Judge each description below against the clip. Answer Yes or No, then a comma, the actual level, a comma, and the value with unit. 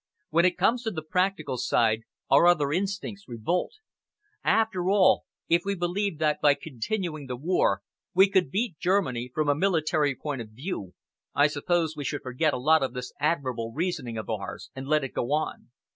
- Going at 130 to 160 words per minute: No, average, 185 wpm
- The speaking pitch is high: No, medium, 155 Hz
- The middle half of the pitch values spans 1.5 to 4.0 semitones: No, wide, 5.6 semitones